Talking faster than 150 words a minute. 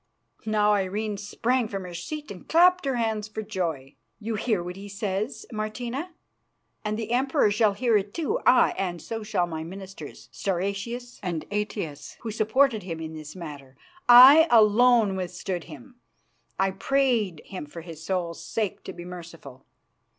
Yes: average, 160 wpm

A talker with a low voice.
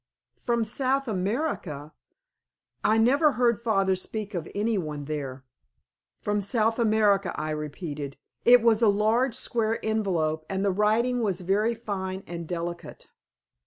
No: high, 205 Hz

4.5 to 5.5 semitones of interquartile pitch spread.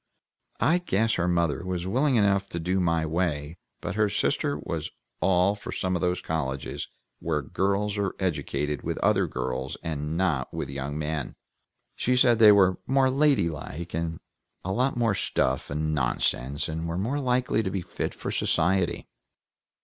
Yes: average, 4.9 semitones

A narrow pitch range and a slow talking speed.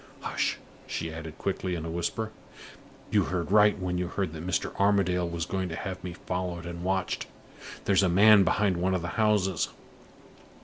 No: narrow, 2.1 semitones; average, 180 wpm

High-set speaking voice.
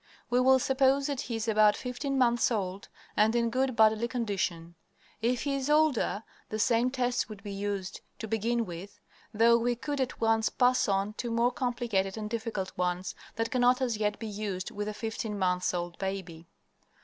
Yes: high, 225 Hz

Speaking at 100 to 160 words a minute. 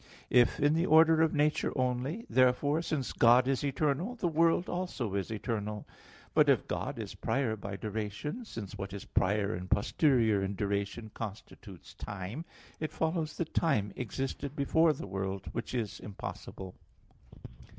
Yes: average, 150 wpm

